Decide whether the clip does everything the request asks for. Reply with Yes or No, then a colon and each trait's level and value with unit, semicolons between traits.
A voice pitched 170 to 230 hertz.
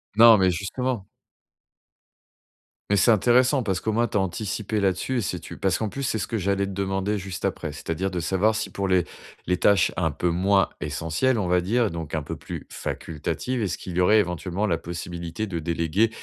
No: very low, 95 Hz